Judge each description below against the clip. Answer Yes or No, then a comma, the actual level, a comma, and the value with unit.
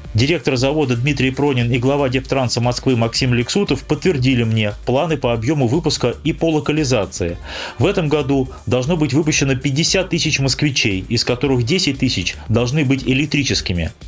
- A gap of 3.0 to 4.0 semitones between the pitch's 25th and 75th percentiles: Yes, average, 3.7 semitones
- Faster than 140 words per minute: Yes, average, 150 wpm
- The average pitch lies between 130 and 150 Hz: Yes, low, 135 Hz